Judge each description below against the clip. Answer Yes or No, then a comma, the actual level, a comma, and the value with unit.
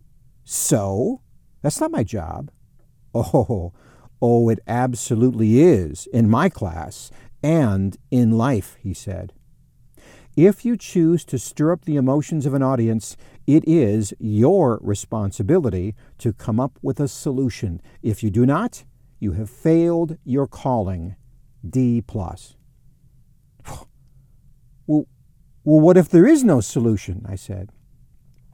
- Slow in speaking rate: Yes, slow, 130 wpm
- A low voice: Yes, low, 125 Hz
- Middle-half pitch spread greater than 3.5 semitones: Yes, average, 4.0 semitones